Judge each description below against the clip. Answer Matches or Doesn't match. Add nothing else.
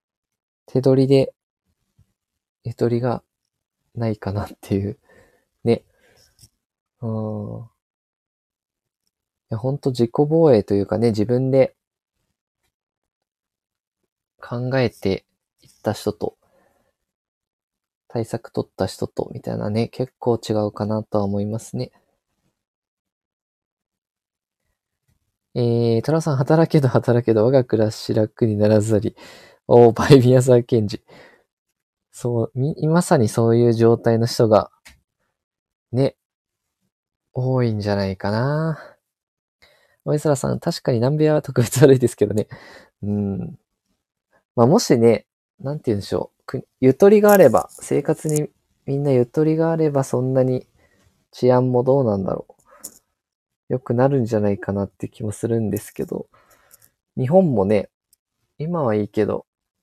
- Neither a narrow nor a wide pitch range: Matches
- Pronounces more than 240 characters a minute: Doesn't match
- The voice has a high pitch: Doesn't match